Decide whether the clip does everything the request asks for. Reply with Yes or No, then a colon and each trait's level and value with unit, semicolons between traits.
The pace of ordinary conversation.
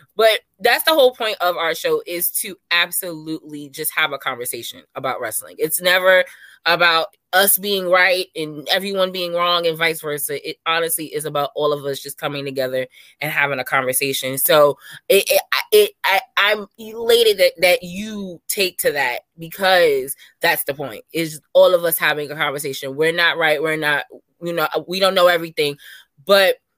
Yes: average, 180 wpm